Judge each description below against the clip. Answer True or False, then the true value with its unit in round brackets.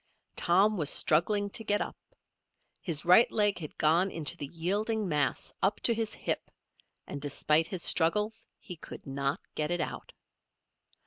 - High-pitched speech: False (175 Hz)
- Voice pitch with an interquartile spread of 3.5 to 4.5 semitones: False (5.3 semitones)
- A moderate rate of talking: True (155 wpm)